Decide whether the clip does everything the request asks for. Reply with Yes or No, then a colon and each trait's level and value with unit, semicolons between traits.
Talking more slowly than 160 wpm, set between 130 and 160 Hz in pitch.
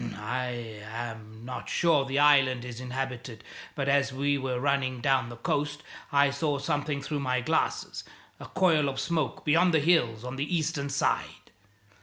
No: average, 165 wpm; low, 135 Hz